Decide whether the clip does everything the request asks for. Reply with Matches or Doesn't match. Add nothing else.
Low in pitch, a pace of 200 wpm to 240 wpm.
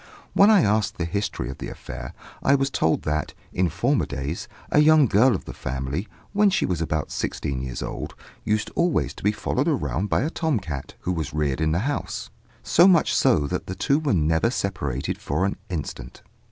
Matches